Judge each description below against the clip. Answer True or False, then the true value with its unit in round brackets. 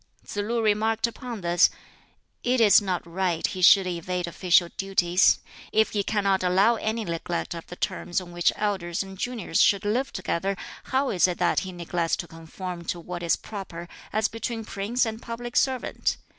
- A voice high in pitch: True (195 Hz)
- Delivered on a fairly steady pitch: False (3.9 semitones)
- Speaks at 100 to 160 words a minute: False (180 wpm)